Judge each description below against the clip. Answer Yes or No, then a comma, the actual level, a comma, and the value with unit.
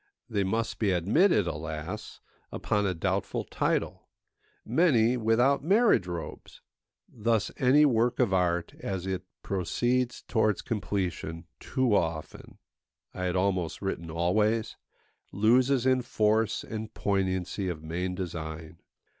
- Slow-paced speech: Yes, slow, 115 wpm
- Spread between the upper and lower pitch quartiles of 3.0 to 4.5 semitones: No, average, 4.9 semitones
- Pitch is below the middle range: Yes, low, 100 Hz